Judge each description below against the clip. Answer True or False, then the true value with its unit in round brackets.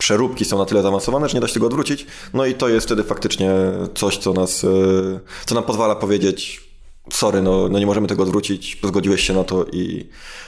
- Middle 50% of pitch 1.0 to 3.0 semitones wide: True (2.5 semitones)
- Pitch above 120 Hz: False (100 Hz)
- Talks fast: True (210 wpm)